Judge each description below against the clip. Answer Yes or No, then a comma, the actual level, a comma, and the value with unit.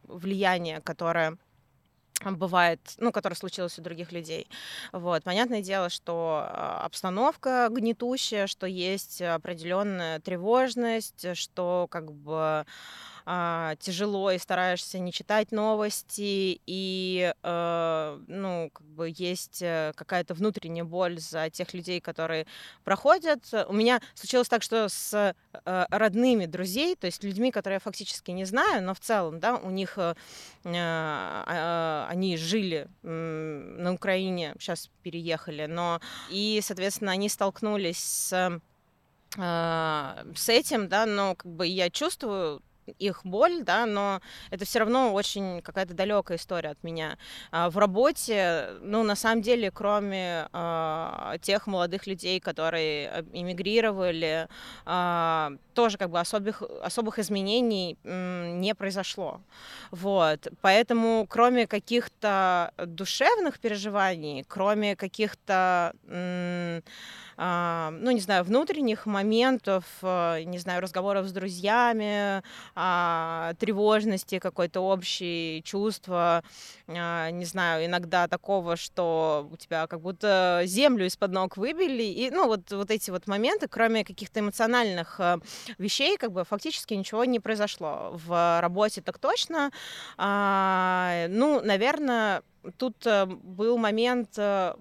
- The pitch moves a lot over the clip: No, average, 3.7 semitones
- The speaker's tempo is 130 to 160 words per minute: No, average, 115 wpm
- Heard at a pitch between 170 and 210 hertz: Yes, high, 190 Hz